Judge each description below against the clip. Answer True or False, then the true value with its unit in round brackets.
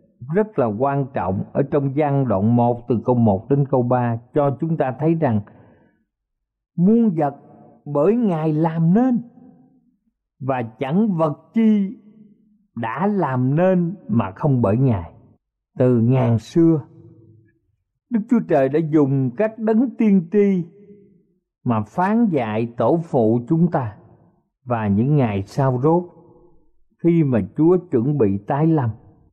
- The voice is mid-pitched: True (150 Hz)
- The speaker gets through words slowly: True (140 wpm)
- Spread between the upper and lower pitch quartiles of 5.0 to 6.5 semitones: False (7.6 semitones)